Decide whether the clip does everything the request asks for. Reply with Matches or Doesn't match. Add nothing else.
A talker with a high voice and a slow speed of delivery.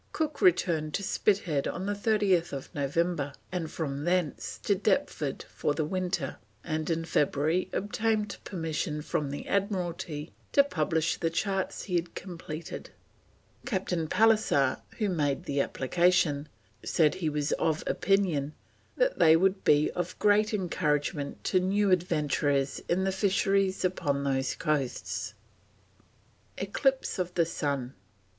Doesn't match